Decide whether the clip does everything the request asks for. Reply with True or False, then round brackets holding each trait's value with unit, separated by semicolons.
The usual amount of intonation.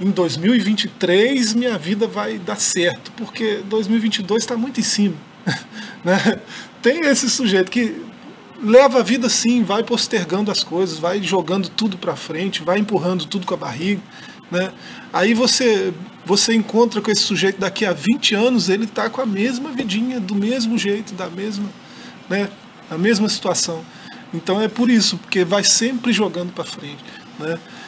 True (3.5 semitones)